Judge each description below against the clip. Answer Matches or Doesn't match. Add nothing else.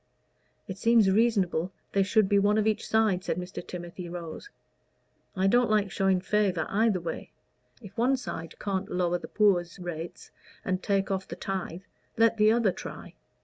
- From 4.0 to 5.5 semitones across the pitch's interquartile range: Doesn't match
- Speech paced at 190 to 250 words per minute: Doesn't match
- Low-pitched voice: Doesn't match